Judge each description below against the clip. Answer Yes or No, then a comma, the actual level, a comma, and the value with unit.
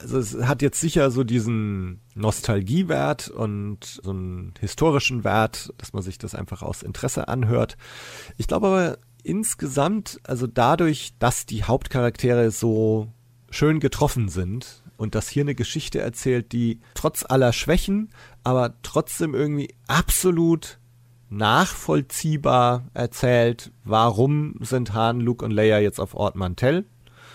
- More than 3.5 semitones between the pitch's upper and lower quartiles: Yes, average, 4.4 semitones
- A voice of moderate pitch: No, low, 120 Hz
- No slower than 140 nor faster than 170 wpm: No, average, 130 wpm